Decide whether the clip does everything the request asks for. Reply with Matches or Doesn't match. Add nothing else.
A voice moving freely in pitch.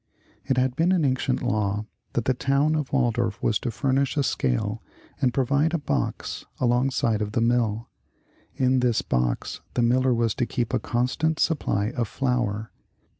Doesn't match